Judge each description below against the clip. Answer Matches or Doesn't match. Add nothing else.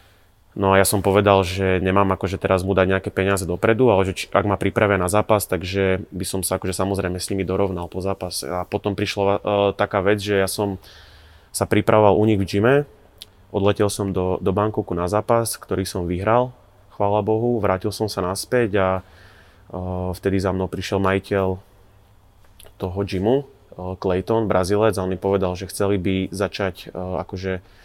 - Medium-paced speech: Doesn't match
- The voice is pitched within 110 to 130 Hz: Doesn't match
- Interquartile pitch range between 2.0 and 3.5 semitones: Doesn't match